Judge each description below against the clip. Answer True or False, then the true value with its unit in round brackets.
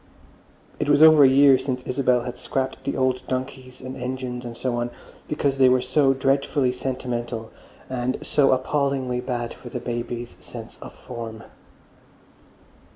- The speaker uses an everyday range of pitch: False (1.6 semitones)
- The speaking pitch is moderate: False (130 Hz)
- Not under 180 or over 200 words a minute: False (155 wpm)